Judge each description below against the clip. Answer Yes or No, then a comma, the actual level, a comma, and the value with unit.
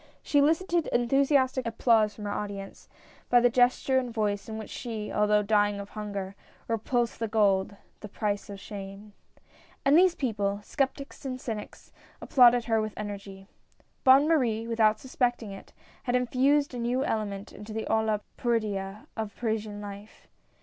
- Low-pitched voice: No, high, 220 Hz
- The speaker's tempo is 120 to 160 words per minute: No, average, 170 wpm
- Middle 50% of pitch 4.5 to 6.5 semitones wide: No, average, 3.3 semitones